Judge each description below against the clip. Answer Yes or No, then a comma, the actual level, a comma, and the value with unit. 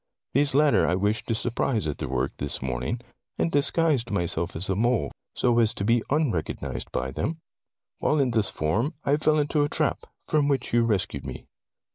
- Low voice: Yes, low, 115 Hz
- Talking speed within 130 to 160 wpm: No, average, 190 wpm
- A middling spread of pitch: No, wide, 9.0 semitones